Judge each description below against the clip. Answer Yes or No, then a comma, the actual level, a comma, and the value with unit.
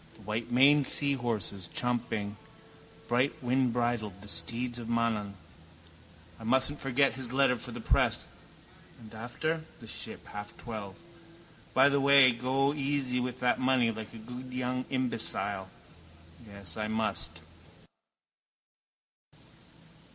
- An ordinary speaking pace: No, slow, 115 wpm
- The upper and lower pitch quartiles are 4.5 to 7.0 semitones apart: No, average, 3.3 semitones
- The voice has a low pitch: Yes, low, 120 Hz